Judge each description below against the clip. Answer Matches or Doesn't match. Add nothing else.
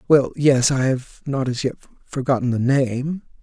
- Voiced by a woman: Doesn't match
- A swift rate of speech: Doesn't match